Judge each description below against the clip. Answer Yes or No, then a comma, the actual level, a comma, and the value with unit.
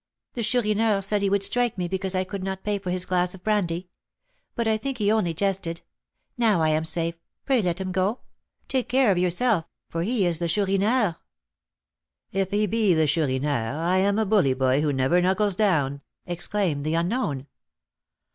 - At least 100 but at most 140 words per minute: No, average, 185 wpm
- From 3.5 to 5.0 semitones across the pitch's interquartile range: Yes, average, 4.0 semitones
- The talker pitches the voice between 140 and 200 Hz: Yes, high, 190 Hz